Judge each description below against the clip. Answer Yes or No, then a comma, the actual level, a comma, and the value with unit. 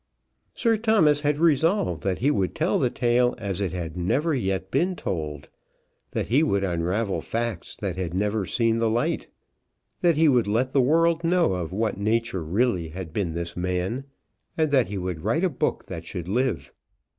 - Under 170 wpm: No, average, 185 wpm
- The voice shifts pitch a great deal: Yes, wide, 7.5 semitones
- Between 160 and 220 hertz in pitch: No, low, 110 Hz